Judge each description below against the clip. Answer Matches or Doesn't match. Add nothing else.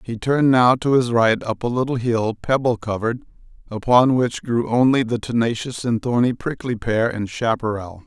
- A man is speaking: Matches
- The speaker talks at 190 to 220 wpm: Doesn't match